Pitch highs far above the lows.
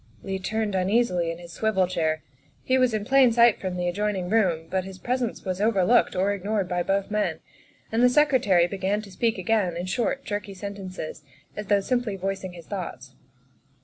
No: average, 3.1 semitones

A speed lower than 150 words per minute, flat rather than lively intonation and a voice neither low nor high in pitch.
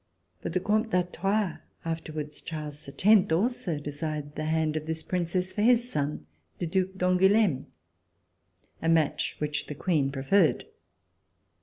No: average, 140 wpm; average, 3.9 semitones; medium, 165 Hz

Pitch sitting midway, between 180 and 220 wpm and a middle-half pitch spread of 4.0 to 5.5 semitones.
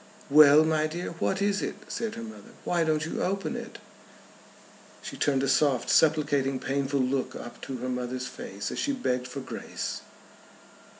No: medium, 145 Hz; average, 170 wpm; average, 4.3 semitones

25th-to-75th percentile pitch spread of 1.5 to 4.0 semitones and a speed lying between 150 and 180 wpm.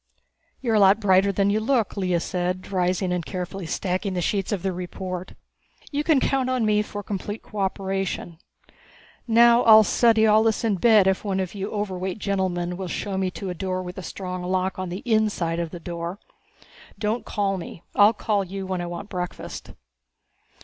No: narrow, 2.6 semitones; average, 190 wpm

